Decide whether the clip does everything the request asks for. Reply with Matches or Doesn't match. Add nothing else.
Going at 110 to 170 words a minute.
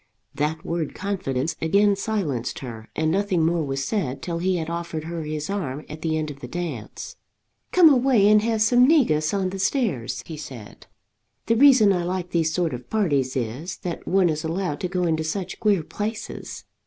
Doesn't match